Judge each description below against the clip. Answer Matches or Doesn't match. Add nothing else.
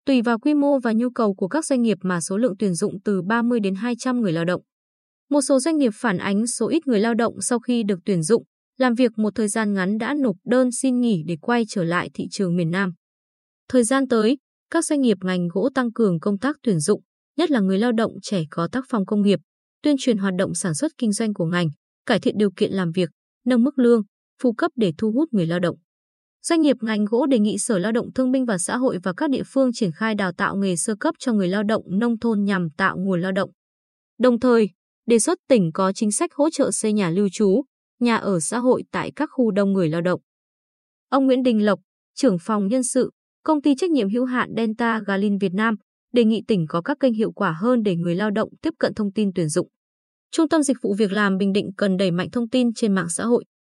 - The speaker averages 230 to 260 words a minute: Matches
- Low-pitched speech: Doesn't match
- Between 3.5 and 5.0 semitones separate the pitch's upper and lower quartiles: Matches